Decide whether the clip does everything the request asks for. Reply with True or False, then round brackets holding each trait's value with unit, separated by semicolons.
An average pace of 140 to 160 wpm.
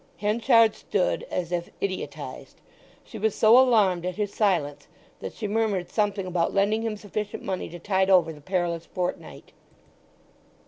True (150 wpm)